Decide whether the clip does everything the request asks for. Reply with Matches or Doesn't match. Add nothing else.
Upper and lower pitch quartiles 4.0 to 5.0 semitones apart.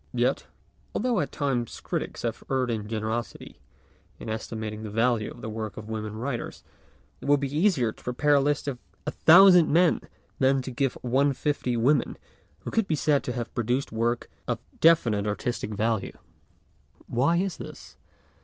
Matches